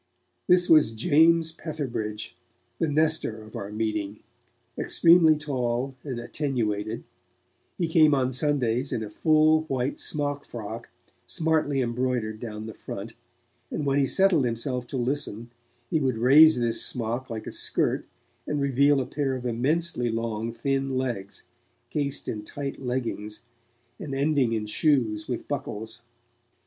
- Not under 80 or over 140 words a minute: Yes, slow, 135 wpm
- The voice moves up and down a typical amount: Yes, average, 4.4 semitones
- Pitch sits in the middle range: No, low, 130 Hz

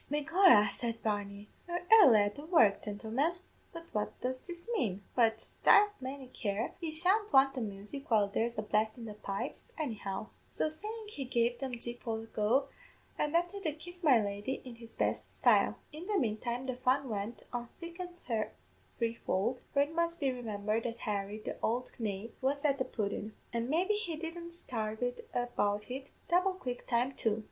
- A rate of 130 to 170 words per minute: No, average, 185 wpm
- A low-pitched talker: No, high, 245 Hz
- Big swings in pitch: Yes, wide, 6.4 semitones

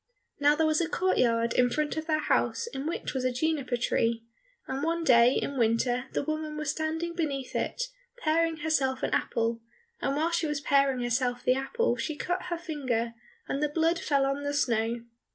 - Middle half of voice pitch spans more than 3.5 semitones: Yes, average, 4.2 semitones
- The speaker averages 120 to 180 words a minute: No, average, 200 wpm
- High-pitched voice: Yes, very high, 285 Hz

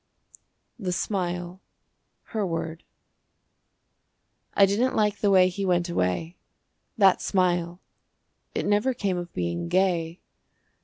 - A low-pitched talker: No, medium, 180 Hz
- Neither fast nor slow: No, slow, 110 wpm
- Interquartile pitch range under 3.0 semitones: Yes, narrow, 2.5 semitones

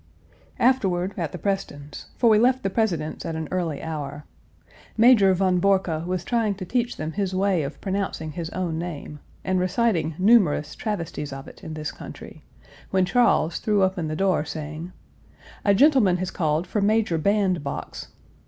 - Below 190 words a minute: Yes, average, 170 wpm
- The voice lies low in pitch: No, medium, 185 Hz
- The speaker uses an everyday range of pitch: Yes, average, 4.1 semitones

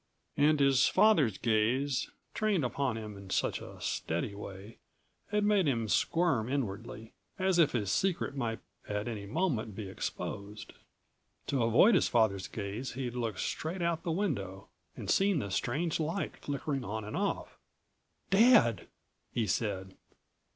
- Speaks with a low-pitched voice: Yes, low, 120 Hz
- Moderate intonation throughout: No, wide, 7.4 semitones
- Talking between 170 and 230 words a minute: No, average, 145 wpm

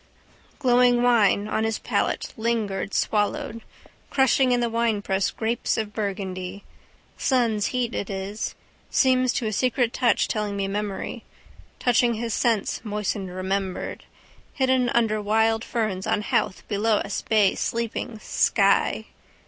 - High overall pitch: Yes, high, 220 Hz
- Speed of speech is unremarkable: No, slow, 130 wpm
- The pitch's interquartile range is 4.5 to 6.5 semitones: No, average, 2.9 semitones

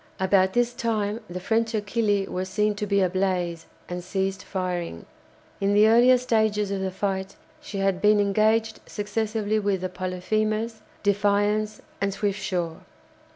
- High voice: Yes, high, 205 Hz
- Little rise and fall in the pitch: Yes, narrow, 2.2 semitones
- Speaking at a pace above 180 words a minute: No, average, 145 wpm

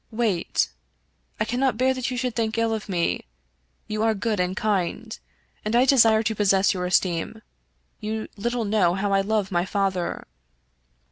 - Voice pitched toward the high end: Yes, high, 215 Hz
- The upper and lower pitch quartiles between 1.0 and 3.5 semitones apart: Yes, average, 2.9 semitones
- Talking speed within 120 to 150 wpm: No, average, 180 wpm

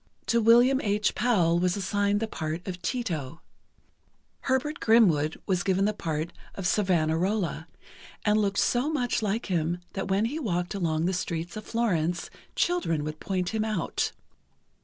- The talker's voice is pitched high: Yes, high, 195 Hz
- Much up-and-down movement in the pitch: No, average, 4.6 semitones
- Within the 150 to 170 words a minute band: Yes, average, 155 wpm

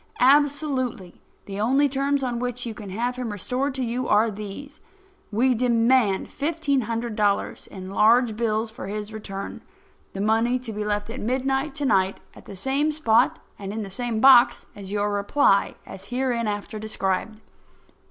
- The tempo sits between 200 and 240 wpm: No, average, 160 wpm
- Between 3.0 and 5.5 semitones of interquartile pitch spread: Yes, average, 3.9 semitones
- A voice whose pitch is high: Yes, high, 230 Hz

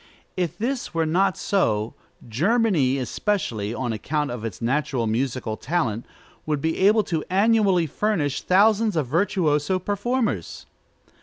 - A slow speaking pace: Yes, slow, 130 wpm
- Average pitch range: No, wide, 8.1 semitones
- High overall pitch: No, medium, 160 Hz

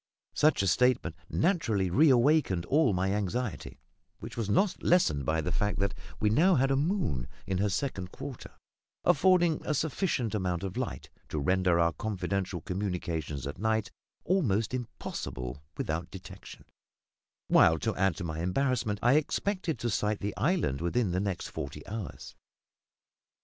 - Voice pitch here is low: Yes, low, 105 Hz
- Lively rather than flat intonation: Yes, wide, 7.0 semitones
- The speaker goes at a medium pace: Yes, average, 150 wpm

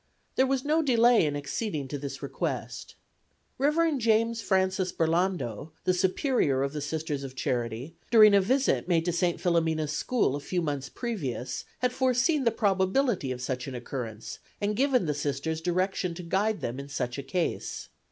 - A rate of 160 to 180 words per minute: Yes, average, 170 wpm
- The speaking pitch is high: No, medium, 175 Hz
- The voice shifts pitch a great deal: Yes, wide, 8.1 semitones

